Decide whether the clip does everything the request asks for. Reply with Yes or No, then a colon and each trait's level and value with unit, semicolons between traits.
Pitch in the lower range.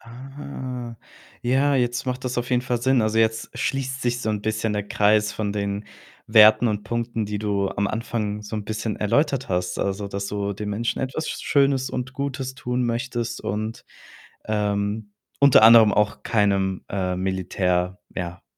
Yes: low, 110 Hz